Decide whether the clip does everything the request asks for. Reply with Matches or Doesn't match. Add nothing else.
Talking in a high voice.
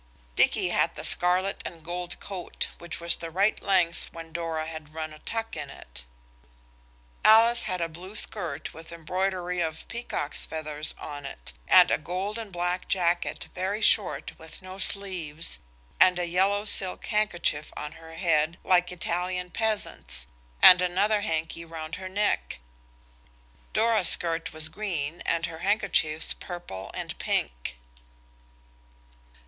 Doesn't match